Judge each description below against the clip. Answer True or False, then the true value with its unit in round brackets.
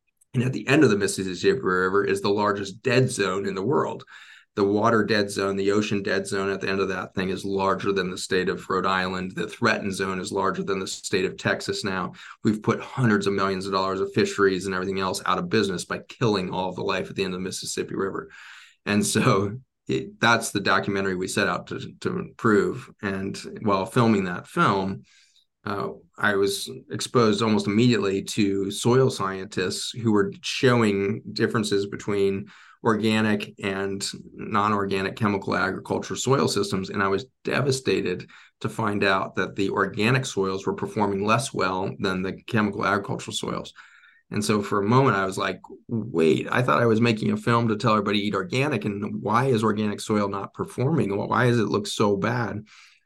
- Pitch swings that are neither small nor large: False (2.0 semitones)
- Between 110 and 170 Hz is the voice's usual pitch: False (100 Hz)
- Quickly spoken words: False (190 wpm)